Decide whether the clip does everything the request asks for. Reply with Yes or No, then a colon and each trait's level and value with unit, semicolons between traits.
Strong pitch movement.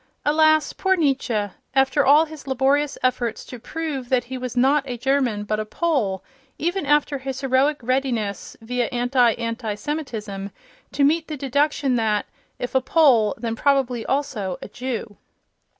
No: average, 3.7 semitones